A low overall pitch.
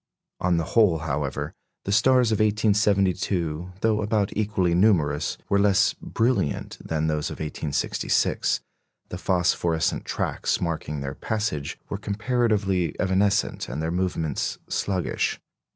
Yes: very low, 95 Hz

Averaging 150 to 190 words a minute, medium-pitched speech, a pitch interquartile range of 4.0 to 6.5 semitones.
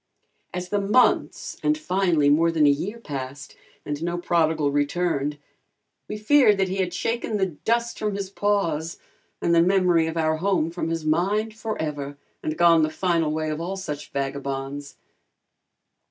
Yes: average, 165 wpm; medium, 170 Hz; average, 4.5 semitones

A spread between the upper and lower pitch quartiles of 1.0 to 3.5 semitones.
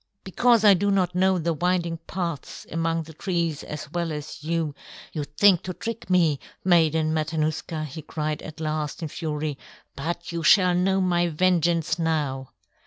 Yes: average, 2.7 semitones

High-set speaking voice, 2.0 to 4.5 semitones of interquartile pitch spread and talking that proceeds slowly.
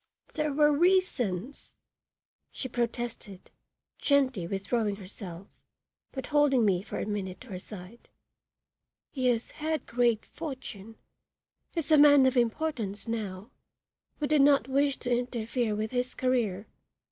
No: high, 245 Hz; average, 5.2 semitones; slow, 130 wpm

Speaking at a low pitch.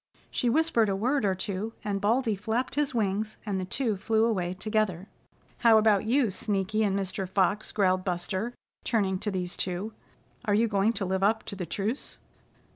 No: high, 205 Hz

